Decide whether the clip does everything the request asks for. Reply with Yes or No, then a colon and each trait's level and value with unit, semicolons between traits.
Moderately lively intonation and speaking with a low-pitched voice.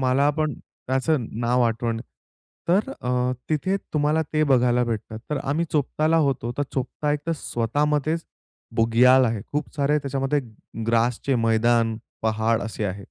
Yes: average, 4.3 semitones; low, 130 Hz